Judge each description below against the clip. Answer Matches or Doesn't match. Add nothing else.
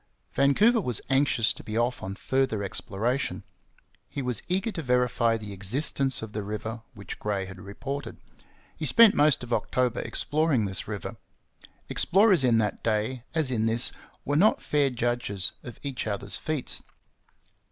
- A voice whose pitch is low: Matches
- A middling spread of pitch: Matches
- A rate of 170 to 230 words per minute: Doesn't match